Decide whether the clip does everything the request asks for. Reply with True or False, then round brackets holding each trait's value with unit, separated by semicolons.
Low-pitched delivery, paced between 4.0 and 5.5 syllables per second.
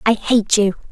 False (215 Hz; 4.4 syllables/s)